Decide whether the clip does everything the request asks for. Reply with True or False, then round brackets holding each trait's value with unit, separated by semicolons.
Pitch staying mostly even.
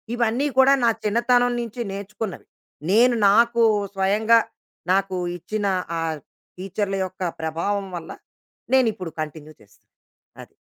False (4.0 semitones)